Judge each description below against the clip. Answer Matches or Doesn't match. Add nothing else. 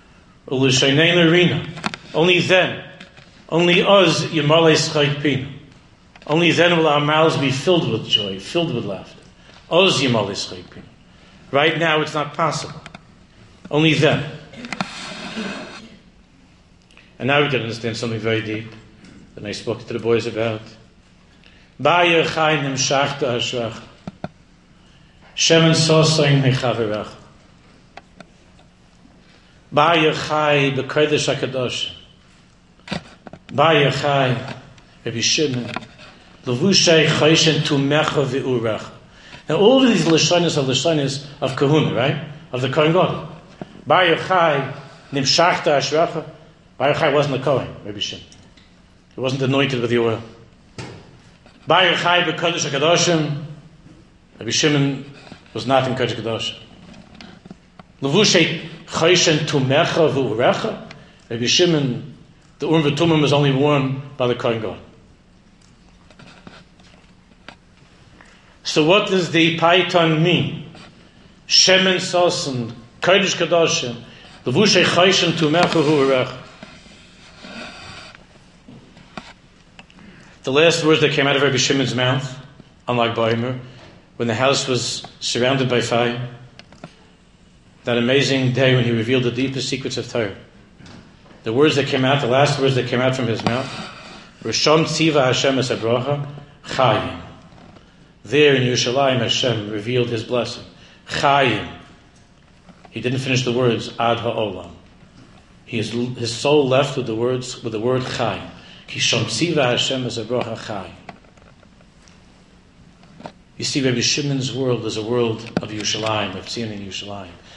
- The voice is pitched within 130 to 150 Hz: Matches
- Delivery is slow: Matches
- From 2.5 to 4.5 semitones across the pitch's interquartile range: Doesn't match